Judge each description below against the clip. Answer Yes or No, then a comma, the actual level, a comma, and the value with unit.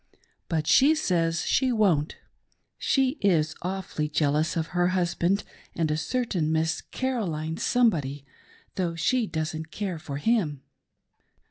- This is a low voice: No, medium, 170 Hz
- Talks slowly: Yes, slow, 125 wpm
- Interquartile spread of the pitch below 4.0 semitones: No, average, 4.9 semitones